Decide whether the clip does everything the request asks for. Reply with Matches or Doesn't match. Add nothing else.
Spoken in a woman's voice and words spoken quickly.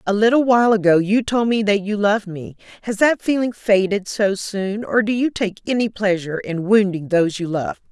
Matches